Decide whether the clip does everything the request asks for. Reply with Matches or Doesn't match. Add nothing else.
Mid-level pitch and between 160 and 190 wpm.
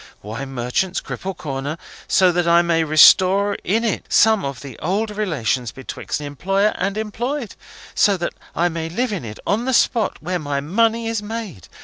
Matches